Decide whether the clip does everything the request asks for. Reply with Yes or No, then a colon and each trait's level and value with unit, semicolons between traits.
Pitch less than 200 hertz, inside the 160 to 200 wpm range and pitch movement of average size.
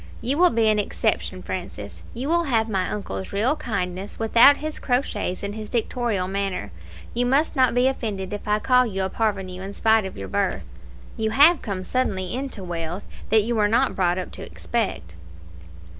No: high, 215 Hz; average, 190 wpm; average, 4.5 semitones